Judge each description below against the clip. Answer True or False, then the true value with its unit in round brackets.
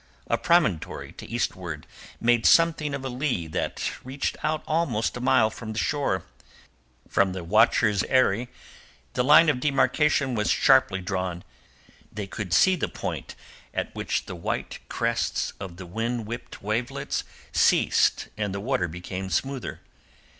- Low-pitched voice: True (115 Hz)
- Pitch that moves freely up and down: True (6.1 semitones)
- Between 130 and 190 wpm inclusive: True (145 wpm)